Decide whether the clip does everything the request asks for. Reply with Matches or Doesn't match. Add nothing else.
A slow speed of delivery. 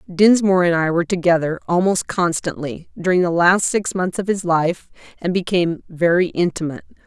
Doesn't match